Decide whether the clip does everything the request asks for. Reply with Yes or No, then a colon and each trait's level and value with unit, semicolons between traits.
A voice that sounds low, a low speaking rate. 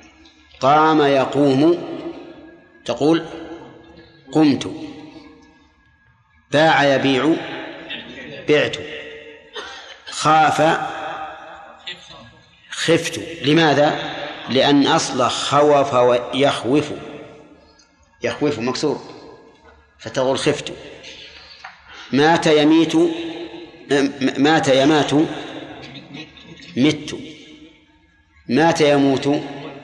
No: medium, 150 Hz; slow, 50 wpm